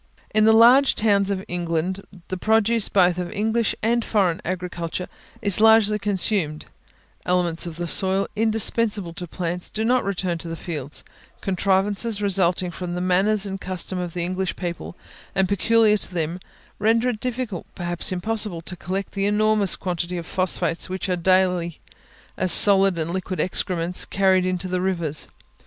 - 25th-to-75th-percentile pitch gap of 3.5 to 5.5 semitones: No, average, 2.9 semitones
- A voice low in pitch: No, medium, 185 Hz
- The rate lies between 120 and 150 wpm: No, average, 160 wpm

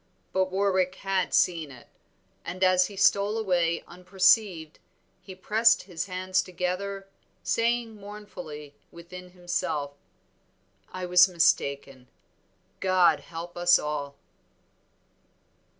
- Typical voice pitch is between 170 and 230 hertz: Yes, medium, 185 Hz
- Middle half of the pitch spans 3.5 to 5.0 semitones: No, narrow, 2.4 semitones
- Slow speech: Yes, slow, 105 wpm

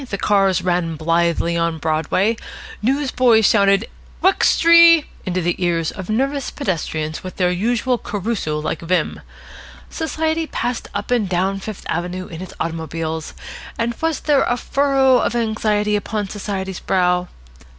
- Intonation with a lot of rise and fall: Yes, wide, 5.7 semitones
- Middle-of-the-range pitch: No, high, 195 Hz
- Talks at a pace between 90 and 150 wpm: Yes, average, 140 wpm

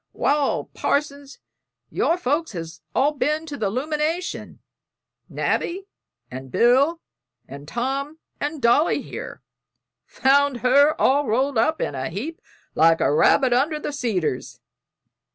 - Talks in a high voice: Yes, very high, 275 Hz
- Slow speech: Yes, slow, 125 wpm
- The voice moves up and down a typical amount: Yes, average, 4.9 semitones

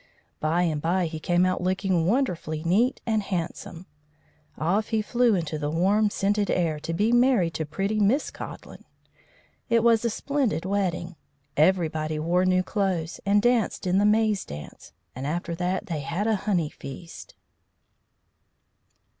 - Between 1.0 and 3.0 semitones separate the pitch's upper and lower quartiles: No, average, 4.2 semitones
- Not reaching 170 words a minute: Yes, average, 155 wpm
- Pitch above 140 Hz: Yes, medium, 185 Hz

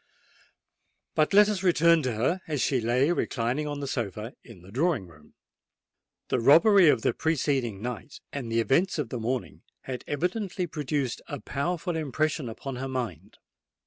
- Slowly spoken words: No, average, 165 wpm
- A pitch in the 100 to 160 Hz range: Yes, medium, 140 Hz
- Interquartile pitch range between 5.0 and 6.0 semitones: Yes, wide, 5.4 semitones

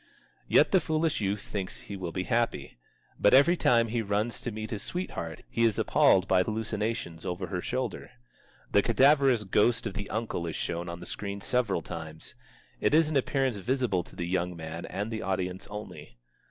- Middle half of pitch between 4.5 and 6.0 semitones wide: Yes, average, 4.8 semitones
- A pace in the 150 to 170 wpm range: No, average, 190 wpm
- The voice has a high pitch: No, low, 105 Hz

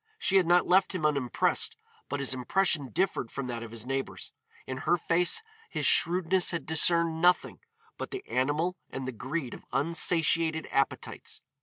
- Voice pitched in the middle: Yes, medium, 160 Hz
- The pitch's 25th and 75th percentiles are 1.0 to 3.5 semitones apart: No, average, 4.9 semitones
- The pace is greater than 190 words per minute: No, average, 165 wpm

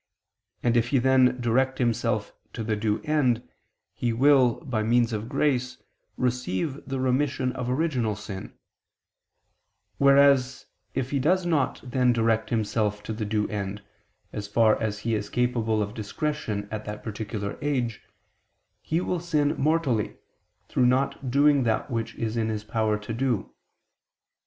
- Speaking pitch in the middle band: No, low, 120 Hz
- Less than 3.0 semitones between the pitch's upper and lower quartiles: No, average, 3.5 semitones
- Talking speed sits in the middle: Yes, average, 150 wpm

